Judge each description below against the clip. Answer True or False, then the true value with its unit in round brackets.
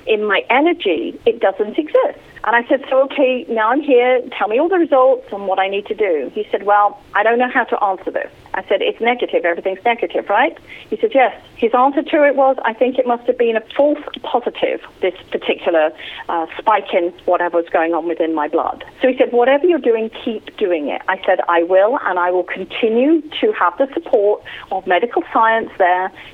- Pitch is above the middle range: True (240 Hz)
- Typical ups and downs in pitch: False (7.1 semitones)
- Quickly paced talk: True (220 wpm)